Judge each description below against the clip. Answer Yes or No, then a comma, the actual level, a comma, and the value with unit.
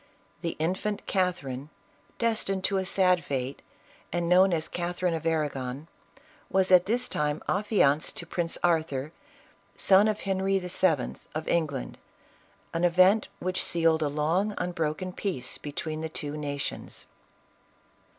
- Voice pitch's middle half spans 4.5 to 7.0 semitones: No, average, 3.8 semitones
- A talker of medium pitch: Yes, medium, 170 Hz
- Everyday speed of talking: No, slow, 130 wpm